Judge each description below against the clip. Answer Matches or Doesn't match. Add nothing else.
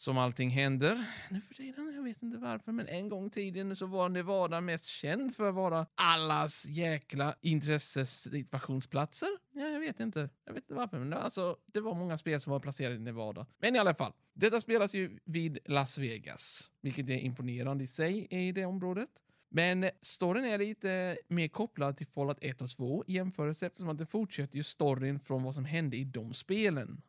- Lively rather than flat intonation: Matches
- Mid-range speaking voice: Matches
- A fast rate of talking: Matches